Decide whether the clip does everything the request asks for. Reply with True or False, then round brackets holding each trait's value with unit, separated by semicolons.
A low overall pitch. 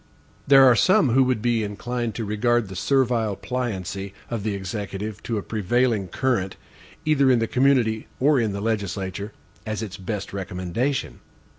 True (110 Hz)